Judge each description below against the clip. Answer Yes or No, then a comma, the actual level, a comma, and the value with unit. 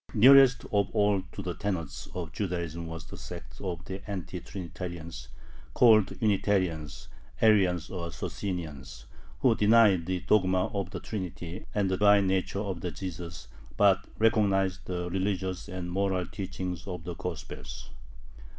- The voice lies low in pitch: Yes, very low, 95 Hz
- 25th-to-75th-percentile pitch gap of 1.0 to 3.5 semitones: Yes, average, 2.8 semitones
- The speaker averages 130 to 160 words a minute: Yes, average, 140 wpm